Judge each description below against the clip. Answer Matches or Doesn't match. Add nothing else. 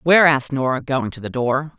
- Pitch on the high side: Doesn't match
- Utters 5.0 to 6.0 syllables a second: Matches